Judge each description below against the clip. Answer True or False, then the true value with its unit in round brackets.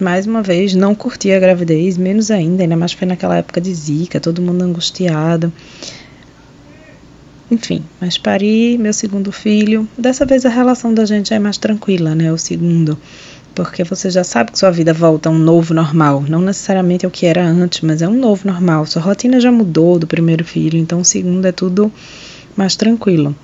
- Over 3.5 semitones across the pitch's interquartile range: True (3.9 semitones)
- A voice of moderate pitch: True (180 Hz)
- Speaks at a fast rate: True (190 wpm)